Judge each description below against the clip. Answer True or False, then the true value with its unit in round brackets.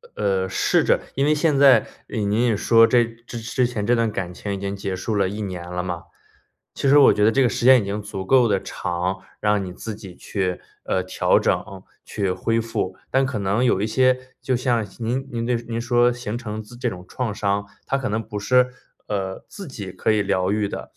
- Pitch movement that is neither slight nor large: True (3.7 semitones)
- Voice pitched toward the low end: True (110 Hz)